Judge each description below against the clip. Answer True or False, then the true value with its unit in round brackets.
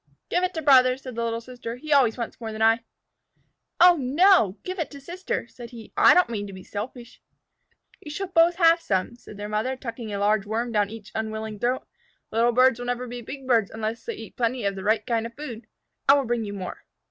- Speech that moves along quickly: True (230 wpm)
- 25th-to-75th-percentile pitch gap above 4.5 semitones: False (3.7 semitones)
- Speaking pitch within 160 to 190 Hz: False (240 Hz)